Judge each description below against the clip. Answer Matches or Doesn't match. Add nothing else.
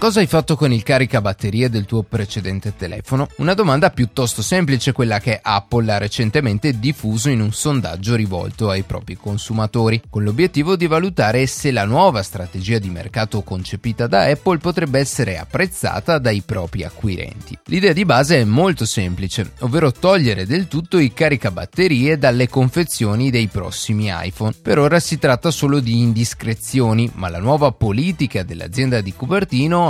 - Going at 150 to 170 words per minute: Matches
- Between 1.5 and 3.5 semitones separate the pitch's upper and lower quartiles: Doesn't match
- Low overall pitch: Matches